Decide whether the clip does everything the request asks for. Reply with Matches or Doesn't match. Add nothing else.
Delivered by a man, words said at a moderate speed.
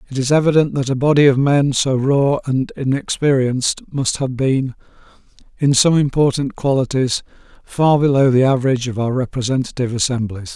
Matches